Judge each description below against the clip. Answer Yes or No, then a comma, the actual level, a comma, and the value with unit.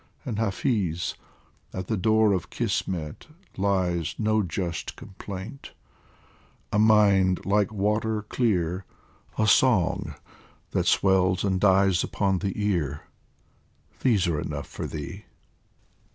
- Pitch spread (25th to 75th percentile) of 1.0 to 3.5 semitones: Yes, average, 2.7 semitones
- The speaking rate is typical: No, slow, 110 wpm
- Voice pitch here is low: Yes, very low, 95 Hz